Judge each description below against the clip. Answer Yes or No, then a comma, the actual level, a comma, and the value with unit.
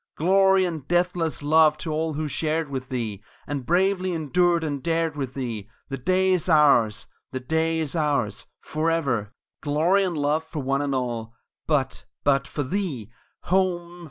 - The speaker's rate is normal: Yes, average, 160 wpm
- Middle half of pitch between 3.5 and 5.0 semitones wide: Yes, average, 4.1 semitones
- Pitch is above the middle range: No, medium, 155 Hz